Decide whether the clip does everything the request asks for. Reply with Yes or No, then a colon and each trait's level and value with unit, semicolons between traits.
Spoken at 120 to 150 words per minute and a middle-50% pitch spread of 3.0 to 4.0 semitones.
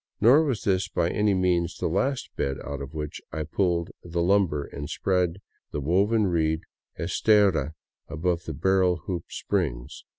No: average, 160 wpm; average, 3.7 semitones